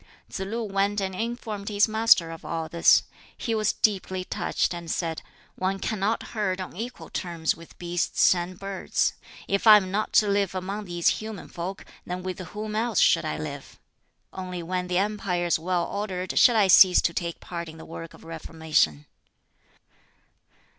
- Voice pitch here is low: No, medium, 185 Hz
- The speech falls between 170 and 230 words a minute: Yes, average, 175 wpm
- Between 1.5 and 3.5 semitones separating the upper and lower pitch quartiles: Yes, average, 3.2 semitones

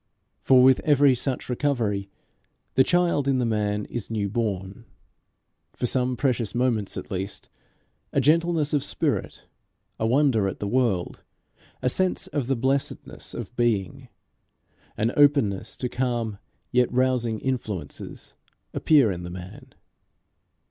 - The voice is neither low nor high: No, low, 125 Hz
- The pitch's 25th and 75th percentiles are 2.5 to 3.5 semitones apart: No, average, 4.3 semitones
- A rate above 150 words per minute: No, slow, 135 wpm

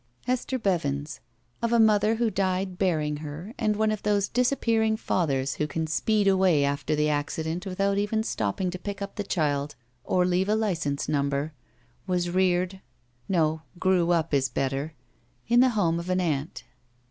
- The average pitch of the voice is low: No, medium, 180 Hz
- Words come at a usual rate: Yes, average, 175 wpm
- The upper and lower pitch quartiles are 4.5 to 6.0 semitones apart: Yes, average, 5.2 semitones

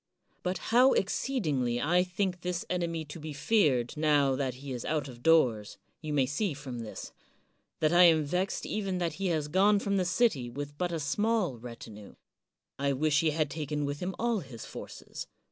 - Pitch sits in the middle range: Yes, medium, 155 Hz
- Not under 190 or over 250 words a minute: Yes, average, 195 wpm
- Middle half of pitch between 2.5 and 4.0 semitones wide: No, average, 4.7 semitones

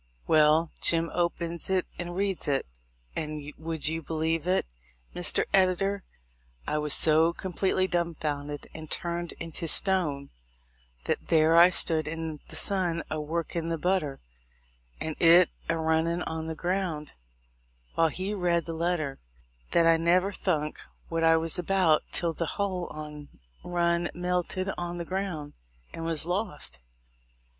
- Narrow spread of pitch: Yes, narrow, 2.1 semitones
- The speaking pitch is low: No, medium, 165 Hz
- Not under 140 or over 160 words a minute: Yes, average, 150 wpm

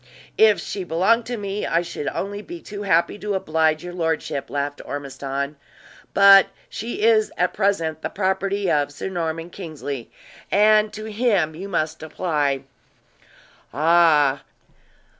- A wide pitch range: No, average, 4.6 semitones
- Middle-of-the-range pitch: Yes, medium, 175 Hz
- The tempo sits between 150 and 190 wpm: No, average, 140 wpm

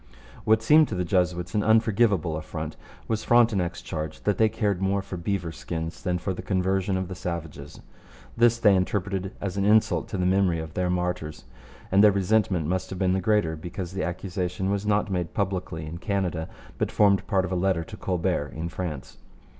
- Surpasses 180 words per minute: Yes, average, 195 wpm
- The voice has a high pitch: No, very low, 95 Hz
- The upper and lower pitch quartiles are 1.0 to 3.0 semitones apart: Yes, narrow, 2.6 semitones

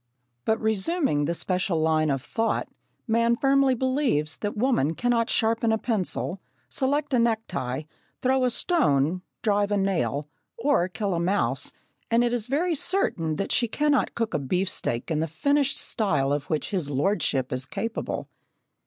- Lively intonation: Yes, wide, 7.6 semitones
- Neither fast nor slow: Yes, average, 160 wpm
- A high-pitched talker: Yes, high, 205 Hz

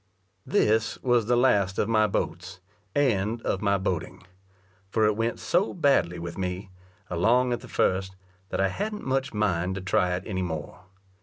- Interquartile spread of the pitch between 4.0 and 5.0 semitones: Yes, average, 4.6 semitones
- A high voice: No, low, 100 Hz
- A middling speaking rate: Yes, average, 170 wpm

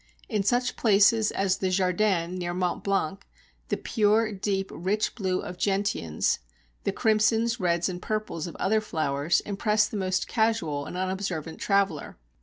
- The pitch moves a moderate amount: Yes, average, 3.2 semitones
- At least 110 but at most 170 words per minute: Yes, average, 150 wpm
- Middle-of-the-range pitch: No, high, 195 Hz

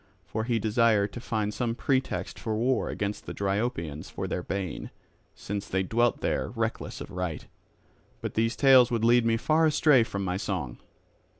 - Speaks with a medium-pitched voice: No, low, 110 Hz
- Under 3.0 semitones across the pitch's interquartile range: No, average, 3.5 semitones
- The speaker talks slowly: No, average, 175 wpm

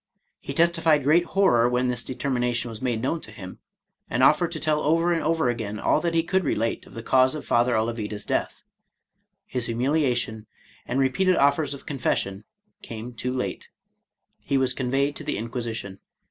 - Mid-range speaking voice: No, low, 130 Hz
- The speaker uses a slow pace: No, average, 190 wpm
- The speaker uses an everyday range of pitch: Yes, average, 4.7 semitones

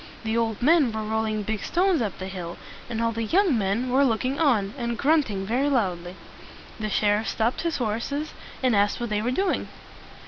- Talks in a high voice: Yes, high, 230 Hz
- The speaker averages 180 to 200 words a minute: Yes, average, 195 wpm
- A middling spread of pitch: Yes, average, 4.2 semitones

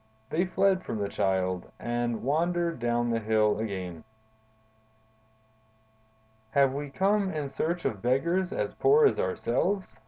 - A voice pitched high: No, low, 135 Hz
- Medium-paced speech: No, slow, 130 wpm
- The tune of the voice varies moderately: No, wide, 8.2 semitones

